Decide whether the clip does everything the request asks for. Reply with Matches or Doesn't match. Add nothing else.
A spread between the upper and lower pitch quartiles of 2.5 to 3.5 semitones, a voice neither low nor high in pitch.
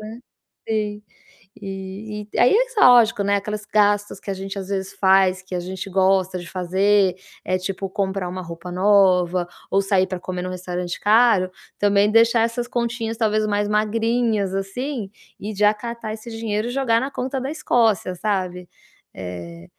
Doesn't match